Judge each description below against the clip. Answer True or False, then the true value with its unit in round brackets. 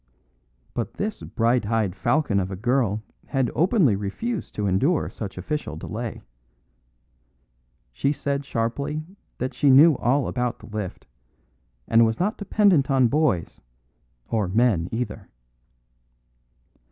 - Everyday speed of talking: False (125 wpm)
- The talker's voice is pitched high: False (120 Hz)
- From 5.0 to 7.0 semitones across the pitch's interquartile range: True (5.5 semitones)